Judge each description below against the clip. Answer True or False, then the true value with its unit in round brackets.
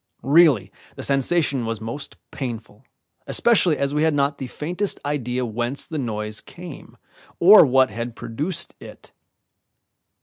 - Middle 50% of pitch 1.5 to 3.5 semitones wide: False (5.0 semitones)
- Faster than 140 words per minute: False (135 wpm)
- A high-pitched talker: False (135 Hz)